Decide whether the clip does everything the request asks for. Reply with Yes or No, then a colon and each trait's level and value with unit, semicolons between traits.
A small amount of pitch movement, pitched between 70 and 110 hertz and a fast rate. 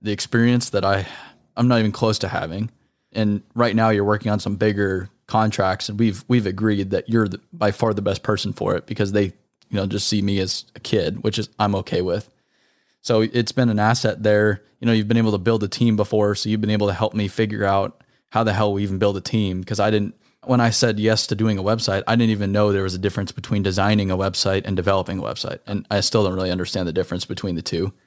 Yes: narrow, 2.0 semitones; low, 105 Hz; fast, 255 wpm